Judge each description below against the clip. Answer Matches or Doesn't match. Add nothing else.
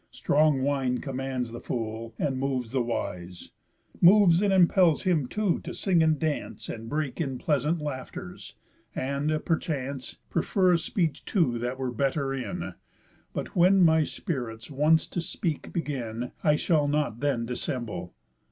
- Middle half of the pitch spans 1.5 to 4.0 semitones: Doesn't match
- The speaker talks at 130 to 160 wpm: Matches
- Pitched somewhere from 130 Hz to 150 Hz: Matches